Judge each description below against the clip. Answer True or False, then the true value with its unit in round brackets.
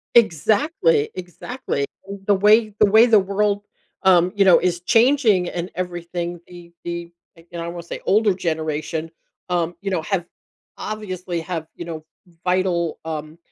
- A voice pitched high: False (180 Hz)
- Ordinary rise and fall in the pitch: True (3.1 semitones)